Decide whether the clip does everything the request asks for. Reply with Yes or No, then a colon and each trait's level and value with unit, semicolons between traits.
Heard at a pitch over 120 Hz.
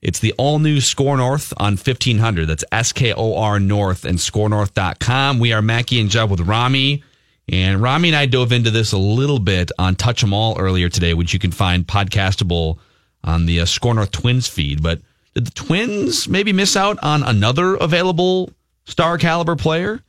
No: low, 110 Hz